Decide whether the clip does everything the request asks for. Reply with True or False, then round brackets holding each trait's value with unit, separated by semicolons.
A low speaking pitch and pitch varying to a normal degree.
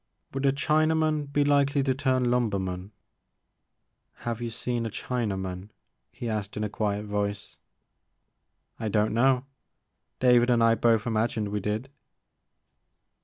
True (115 Hz; 4.1 semitones)